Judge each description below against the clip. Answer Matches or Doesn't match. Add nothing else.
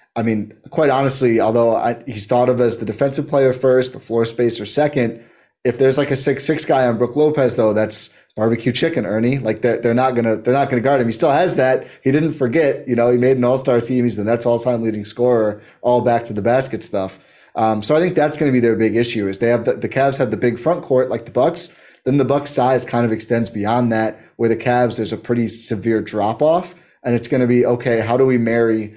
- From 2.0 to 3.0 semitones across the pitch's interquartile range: Matches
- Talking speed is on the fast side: Matches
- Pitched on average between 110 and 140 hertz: Matches